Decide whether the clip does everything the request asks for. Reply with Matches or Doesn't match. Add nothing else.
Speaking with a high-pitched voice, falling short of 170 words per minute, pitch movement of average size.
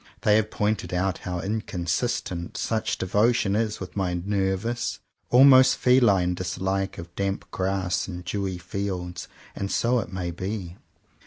Doesn't match